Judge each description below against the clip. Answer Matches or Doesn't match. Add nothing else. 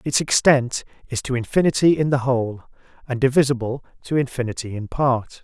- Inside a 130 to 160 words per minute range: Matches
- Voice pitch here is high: Doesn't match